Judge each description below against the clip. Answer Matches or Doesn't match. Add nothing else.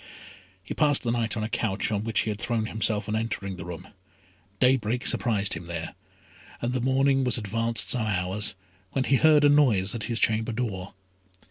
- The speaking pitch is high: Doesn't match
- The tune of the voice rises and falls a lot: Doesn't match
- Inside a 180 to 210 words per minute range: Matches